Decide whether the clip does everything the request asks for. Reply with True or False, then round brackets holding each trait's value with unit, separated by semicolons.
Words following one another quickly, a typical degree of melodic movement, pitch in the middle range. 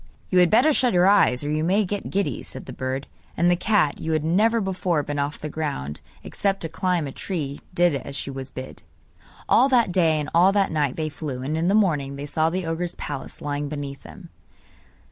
True (220 wpm; 4.5 semitones; 160 Hz)